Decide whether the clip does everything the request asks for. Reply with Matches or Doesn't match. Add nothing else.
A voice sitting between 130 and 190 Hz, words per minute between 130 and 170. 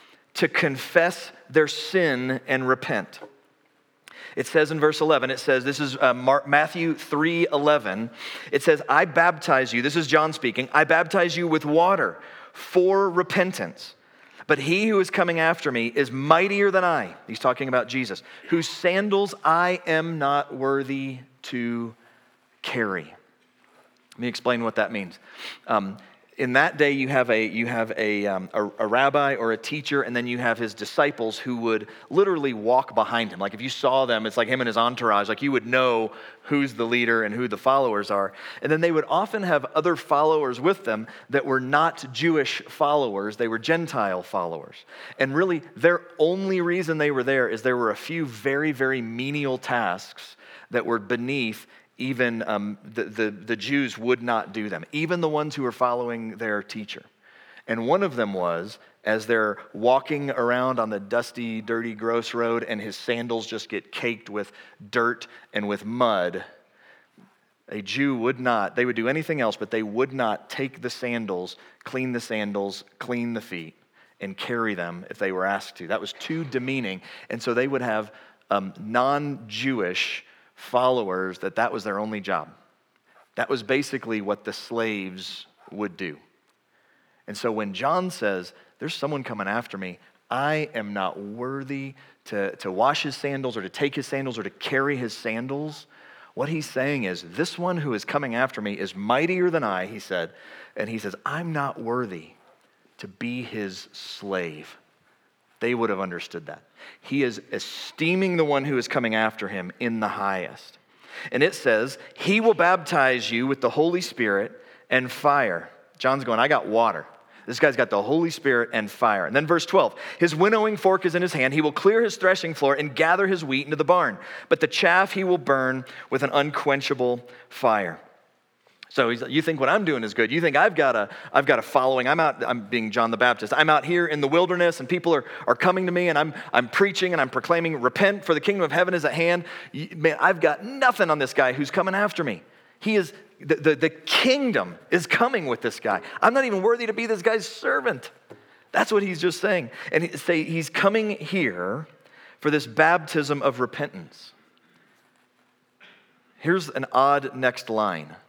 Doesn't match